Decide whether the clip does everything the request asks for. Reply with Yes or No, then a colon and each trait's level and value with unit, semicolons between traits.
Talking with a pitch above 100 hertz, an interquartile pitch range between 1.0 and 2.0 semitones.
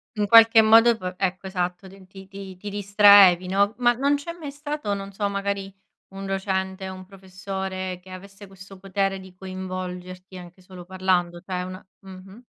Yes: high, 190 Hz; narrow, 1.4 semitones